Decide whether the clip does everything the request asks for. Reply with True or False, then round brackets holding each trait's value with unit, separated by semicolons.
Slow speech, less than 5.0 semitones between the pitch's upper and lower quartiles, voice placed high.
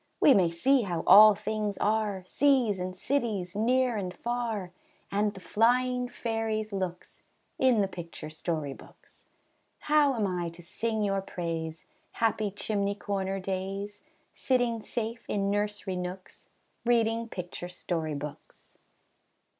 True (130 wpm; 3.8 semitones; 205 Hz)